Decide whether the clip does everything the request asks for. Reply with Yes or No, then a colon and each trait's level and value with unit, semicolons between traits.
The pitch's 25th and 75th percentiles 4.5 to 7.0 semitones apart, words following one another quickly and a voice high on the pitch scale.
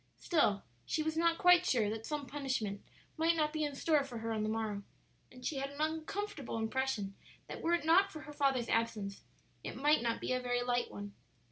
Yes: wide, 5.6 semitones; fast, 215 wpm; very high, 270 Hz